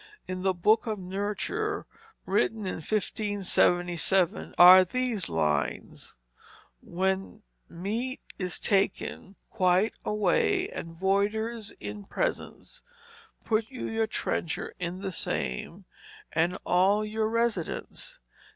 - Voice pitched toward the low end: No, high, 195 Hz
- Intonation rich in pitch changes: No, average, 3.3 semitones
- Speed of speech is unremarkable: No, slow, 105 wpm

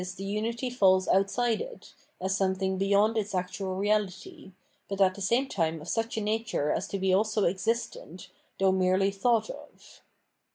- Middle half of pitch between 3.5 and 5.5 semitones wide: No, average, 2.8 semitones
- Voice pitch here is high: Yes, high, 195 Hz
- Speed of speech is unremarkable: Yes, average, 165 wpm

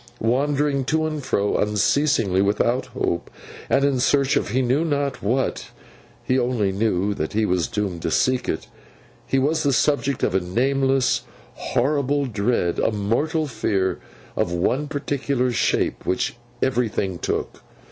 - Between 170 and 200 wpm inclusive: No, average, 145 wpm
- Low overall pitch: Yes, low, 125 Hz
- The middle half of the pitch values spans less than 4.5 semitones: No, average, 5.3 semitones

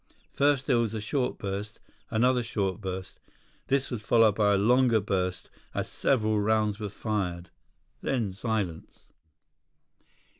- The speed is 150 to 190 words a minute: No, slow, 135 wpm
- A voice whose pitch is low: Yes, low, 110 Hz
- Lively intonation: No, average, 3.3 semitones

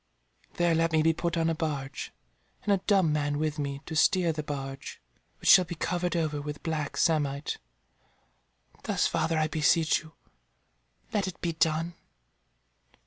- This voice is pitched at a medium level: Yes, medium, 160 Hz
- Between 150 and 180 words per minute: Yes, average, 160 wpm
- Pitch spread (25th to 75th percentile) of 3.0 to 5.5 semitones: No, narrow, 2.4 semitones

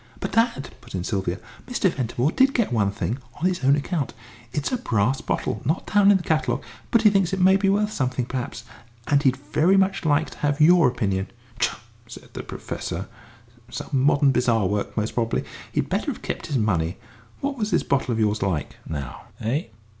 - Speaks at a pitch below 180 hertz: Yes, medium, 140 Hz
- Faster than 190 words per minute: Yes, average, 200 wpm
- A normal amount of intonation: No, wide, 8.7 semitones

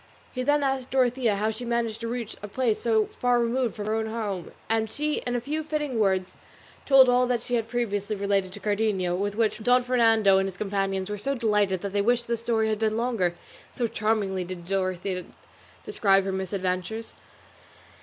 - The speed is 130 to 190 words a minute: No, average, 200 wpm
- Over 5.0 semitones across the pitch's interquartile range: No, average, 3.6 semitones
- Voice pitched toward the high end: Yes, high, 220 Hz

